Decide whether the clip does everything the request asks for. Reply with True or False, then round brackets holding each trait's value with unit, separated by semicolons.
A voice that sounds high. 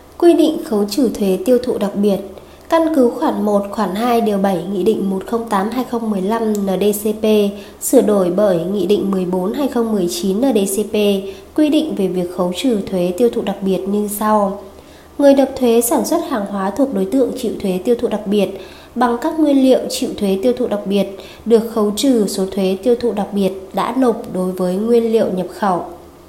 True (210 Hz)